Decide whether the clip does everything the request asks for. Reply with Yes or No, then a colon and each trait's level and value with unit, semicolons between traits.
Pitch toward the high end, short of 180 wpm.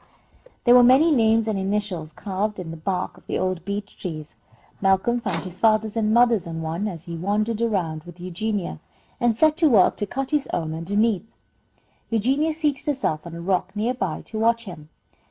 No: high, 205 Hz; average, 190 wpm